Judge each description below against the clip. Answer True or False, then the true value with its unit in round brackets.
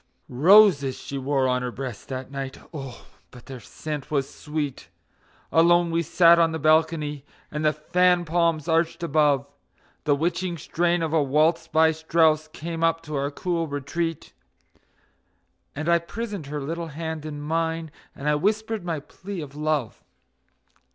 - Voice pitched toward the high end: False (155 Hz)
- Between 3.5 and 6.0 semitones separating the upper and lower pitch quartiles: False (2.7 semitones)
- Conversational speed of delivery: True (160 wpm)